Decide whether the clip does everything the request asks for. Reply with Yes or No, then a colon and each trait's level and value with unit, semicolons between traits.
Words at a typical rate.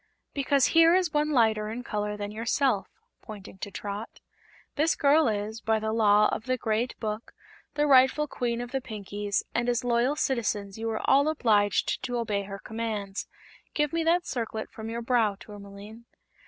Yes: average, 175 wpm